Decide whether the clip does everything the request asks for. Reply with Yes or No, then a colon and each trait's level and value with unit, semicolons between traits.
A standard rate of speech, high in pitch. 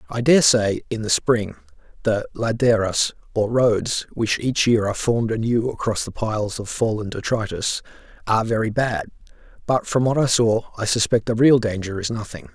No: average, 175 wpm; low, 110 Hz